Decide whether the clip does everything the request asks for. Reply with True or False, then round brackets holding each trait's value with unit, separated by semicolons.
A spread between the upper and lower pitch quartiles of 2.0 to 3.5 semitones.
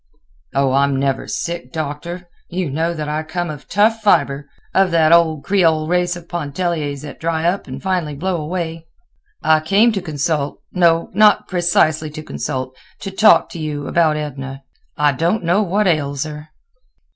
True (3.1 semitones)